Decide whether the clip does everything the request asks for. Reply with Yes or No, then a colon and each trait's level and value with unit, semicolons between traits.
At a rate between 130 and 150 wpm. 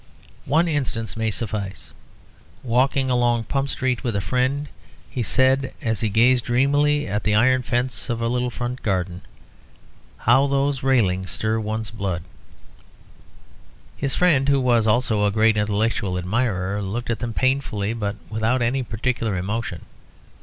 Yes: average, 145 wpm